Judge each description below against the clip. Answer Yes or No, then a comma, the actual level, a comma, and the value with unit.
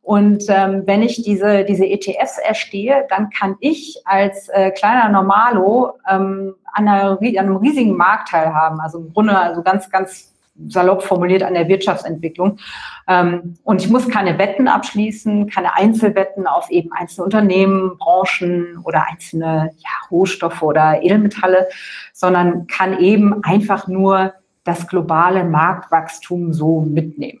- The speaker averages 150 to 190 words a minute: No, average, 140 wpm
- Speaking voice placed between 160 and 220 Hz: Yes, high, 190 Hz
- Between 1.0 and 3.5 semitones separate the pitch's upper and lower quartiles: Yes, narrow, 2.6 semitones